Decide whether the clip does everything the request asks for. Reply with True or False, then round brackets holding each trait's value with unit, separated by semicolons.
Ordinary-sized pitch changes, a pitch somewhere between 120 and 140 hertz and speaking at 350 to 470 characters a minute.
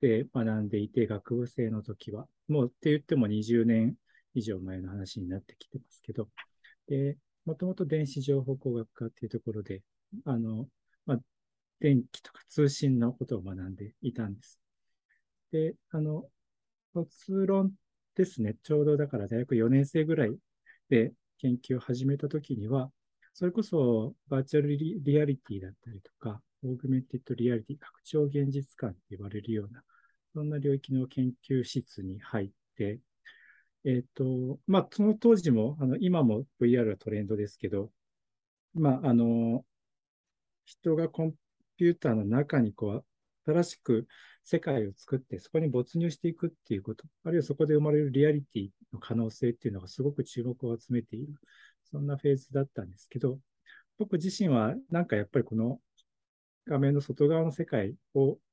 False (4.9 semitones; 130 Hz; 320 characters per minute)